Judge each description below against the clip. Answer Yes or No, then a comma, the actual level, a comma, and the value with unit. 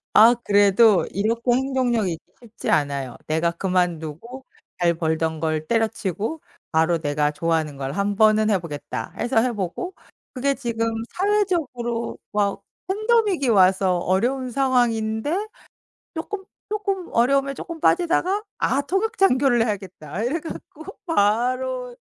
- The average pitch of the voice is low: No, high, 230 Hz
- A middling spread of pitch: No, wide, 7.4 semitones